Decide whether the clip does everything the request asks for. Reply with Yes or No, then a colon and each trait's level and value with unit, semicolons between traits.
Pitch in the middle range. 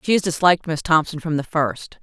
Yes: medium, 160 Hz